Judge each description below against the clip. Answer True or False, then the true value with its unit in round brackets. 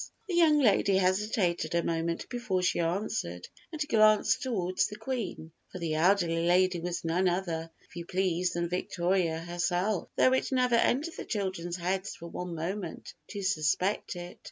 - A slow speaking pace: False (165 wpm)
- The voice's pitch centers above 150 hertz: True (185 Hz)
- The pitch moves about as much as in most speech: True (3.5 semitones)